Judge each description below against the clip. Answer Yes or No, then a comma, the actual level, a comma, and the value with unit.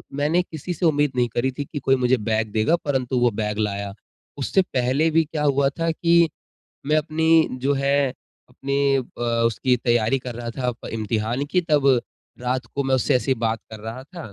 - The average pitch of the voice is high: No, low, 135 Hz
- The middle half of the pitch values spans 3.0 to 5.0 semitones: Yes, average, 3.8 semitones